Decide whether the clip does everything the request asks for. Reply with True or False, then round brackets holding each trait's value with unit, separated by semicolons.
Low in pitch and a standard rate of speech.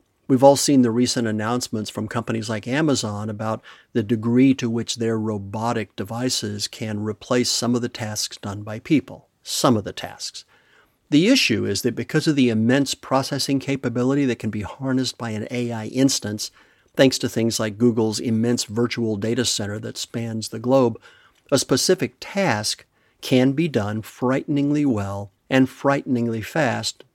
True (120 Hz; 160 wpm)